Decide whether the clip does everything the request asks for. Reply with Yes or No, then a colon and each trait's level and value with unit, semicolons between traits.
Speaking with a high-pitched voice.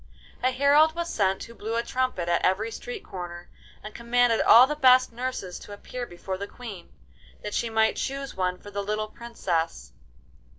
Yes: high, 225 Hz